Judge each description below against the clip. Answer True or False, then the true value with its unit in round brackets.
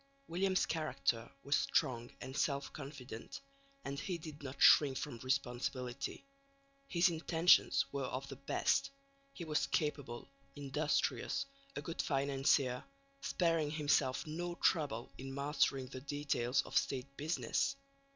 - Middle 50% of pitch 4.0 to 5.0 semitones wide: False (2.9 semitones)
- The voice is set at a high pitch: False (140 Hz)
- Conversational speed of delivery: False (125 wpm)